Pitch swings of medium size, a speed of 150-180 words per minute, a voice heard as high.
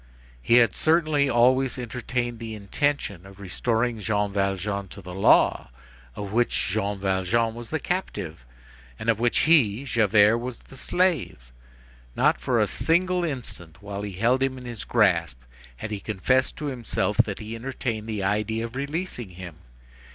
No: average, 4.5 semitones; average, 160 wpm; low, 115 Hz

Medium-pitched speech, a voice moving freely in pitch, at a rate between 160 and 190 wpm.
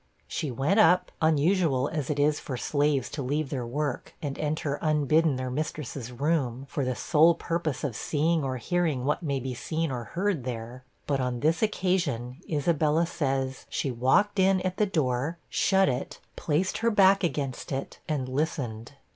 No: medium, 145 Hz; average, 4.2 semitones; average, 170 wpm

